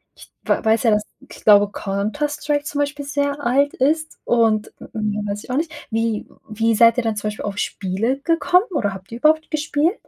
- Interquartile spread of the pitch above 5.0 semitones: Yes, wide, 5.5 semitones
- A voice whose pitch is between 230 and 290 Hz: Yes, high, 235 Hz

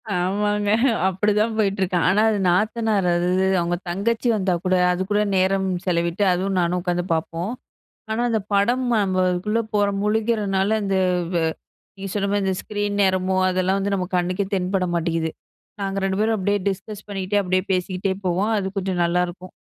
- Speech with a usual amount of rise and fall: No, narrow, 2.2 semitones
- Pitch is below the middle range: No, high, 190 Hz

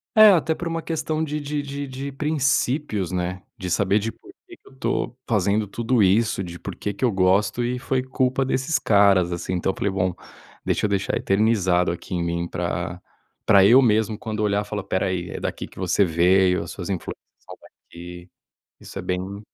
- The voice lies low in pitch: Yes, low, 105 Hz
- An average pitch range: No, wide, 6.0 semitones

